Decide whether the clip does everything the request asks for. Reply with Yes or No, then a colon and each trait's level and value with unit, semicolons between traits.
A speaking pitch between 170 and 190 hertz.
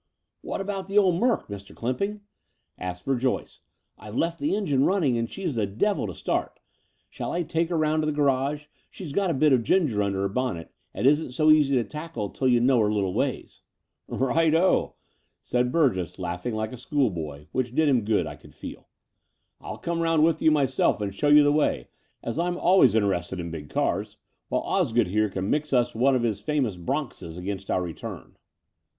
No: low, 130 Hz